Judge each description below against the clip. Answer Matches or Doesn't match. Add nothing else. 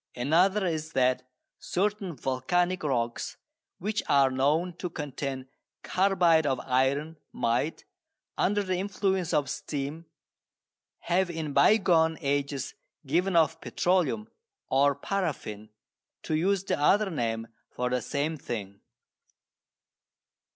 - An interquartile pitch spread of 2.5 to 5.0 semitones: Doesn't match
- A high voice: Doesn't match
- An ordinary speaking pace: Doesn't match